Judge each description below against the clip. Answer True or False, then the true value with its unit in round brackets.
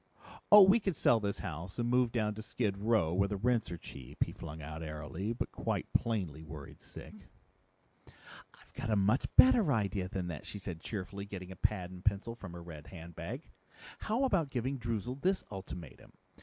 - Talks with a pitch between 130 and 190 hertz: False (100 Hz)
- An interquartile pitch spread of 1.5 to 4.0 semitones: False (5.1 semitones)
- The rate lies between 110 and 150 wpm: False (190 wpm)